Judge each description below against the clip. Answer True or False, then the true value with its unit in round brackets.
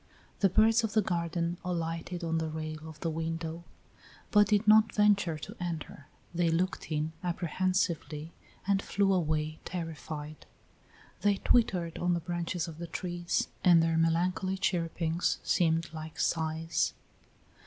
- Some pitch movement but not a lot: False (2.3 semitones)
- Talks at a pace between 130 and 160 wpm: True (140 wpm)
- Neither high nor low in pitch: True (170 Hz)